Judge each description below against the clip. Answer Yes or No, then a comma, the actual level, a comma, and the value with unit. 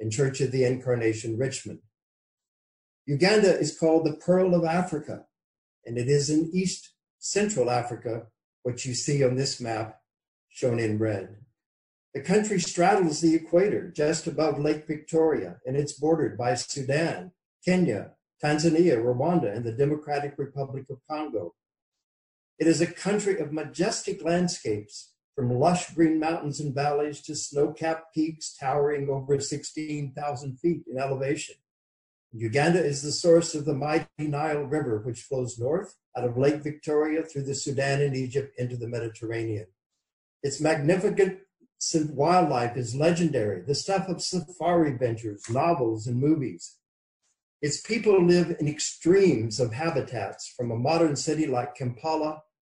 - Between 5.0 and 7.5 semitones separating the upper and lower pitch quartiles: No, average, 4.6 semitones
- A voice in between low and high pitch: Yes, medium, 145 Hz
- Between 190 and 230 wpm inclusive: No, average, 140 wpm